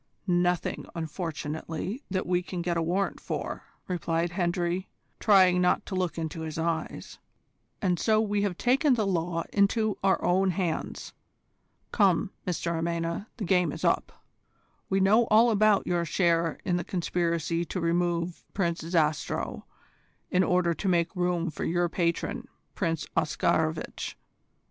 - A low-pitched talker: No, medium, 175 Hz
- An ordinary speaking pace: Yes, average, 145 wpm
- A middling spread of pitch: No, narrow, 2.3 semitones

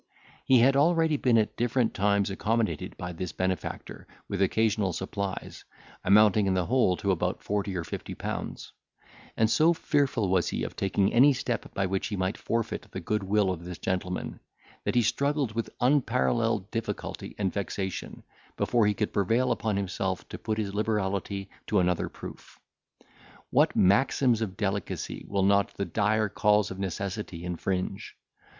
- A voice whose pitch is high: No, low, 100 Hz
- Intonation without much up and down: No, average, 3.1 semitones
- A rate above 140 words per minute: Yes, average, 160 wpm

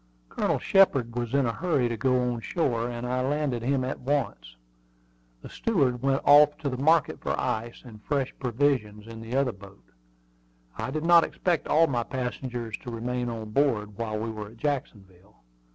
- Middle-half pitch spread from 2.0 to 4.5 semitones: Yes, average, 3.6 semitones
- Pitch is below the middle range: Yes, low, 125 Hz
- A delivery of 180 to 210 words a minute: Yes, average, 185 wpm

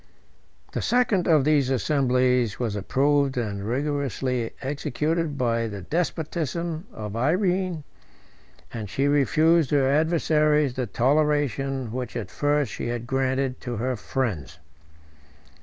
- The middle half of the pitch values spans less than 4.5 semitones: Yes, average, 3.9 semitones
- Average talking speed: No, slow, 120 wpm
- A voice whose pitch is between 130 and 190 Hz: Yes, low, 135 Hz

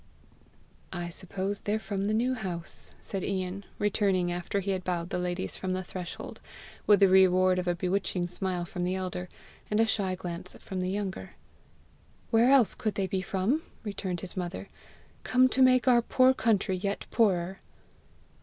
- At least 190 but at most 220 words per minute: No, average, 175 wpm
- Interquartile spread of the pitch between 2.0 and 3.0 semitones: Yes, narrow, 2.4 semitones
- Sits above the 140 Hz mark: Yes, high, 190 Hz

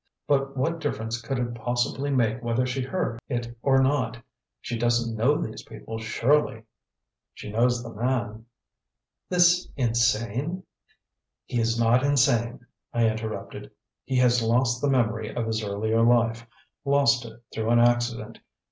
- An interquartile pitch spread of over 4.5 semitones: No, narrow, 2.5 semitones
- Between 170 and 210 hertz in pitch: No, low, 120 Hz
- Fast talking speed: No, average, 145 wpm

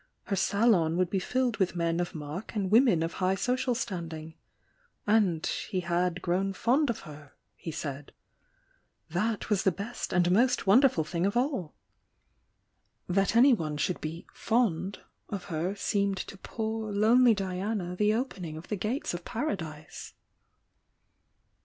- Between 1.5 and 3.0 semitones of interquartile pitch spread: No, average, 4.5 semitones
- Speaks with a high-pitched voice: Yes, high, 195 Hz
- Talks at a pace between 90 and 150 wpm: Yes, average, 145 wpm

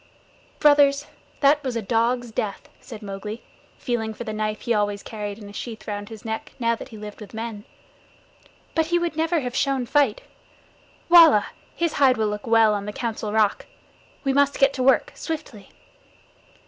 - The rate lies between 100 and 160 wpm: No, average, 175 wpm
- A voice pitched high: Yes, high, 230 Hz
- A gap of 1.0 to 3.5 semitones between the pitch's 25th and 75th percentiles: No, average, 4.5 semitones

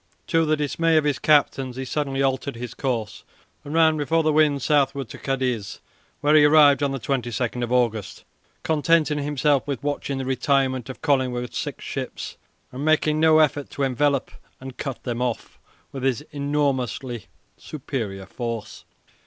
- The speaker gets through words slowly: No, average, 155 wpm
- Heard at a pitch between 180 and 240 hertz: No, medium, 140 Hz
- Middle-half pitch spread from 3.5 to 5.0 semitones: No, average, 2.8 semitones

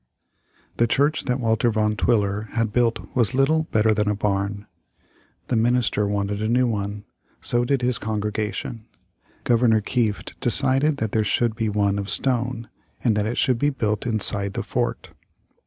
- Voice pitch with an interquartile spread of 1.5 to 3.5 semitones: Yes, average, 2.8 semitones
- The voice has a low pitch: Yes, low, 110 Hz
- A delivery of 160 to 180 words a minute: Yes, average, 165 wpm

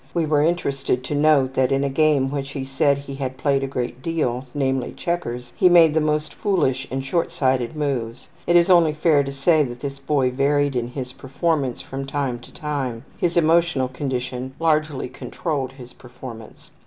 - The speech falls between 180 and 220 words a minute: Yes, average, 185 wpm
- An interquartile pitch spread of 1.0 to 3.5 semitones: Yes, average, 2.8 semitones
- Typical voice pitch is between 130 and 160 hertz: Yes, medium, 140 Hz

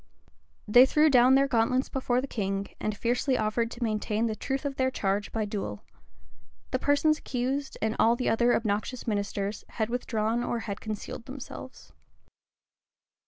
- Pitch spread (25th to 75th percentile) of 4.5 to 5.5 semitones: No, average, 3.4 semitones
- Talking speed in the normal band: Yes, average, 160 wpm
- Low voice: No, high, 235 Hz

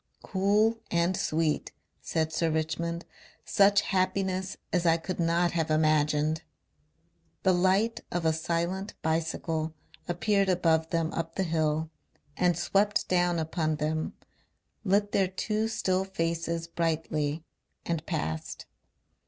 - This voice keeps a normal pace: No, slow, 120 wpm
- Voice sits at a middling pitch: Yes, medium, 170 Hz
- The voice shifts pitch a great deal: No, average, 2.9 semitones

